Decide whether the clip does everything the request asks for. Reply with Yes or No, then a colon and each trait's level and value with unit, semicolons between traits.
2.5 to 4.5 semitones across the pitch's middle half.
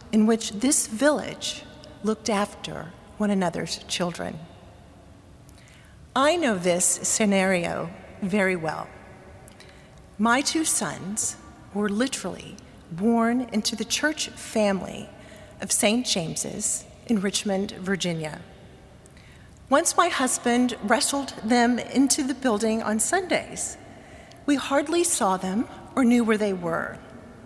Yes: average, 4.2 semitones